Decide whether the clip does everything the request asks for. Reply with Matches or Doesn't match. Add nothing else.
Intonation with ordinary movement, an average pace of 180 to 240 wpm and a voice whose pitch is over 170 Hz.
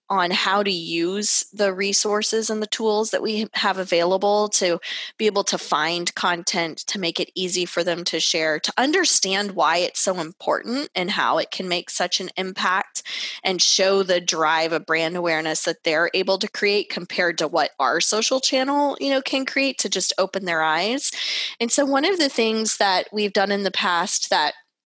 Matches